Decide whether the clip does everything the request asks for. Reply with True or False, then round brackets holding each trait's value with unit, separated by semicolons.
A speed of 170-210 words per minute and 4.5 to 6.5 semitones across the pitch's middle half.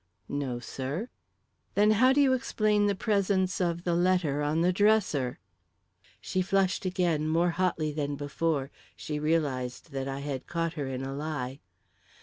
False (155 wpm; 4.8 semitones)